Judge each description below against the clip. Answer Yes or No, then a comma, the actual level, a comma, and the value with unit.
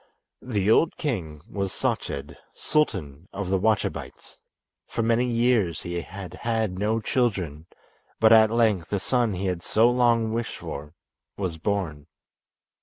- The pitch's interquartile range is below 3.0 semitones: No, average, 4.5 semitones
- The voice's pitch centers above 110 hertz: No, low, 100 Hz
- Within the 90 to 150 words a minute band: Yes, average, 140 wpm